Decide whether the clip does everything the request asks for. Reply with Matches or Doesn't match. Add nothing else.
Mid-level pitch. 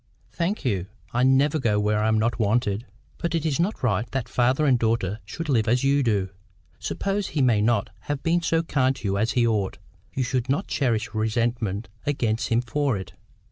Doesn't match